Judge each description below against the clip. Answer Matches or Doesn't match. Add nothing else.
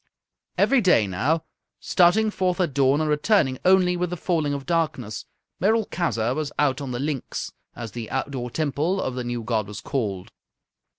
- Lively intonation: Matches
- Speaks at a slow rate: Doesn't match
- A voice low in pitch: Doesn't match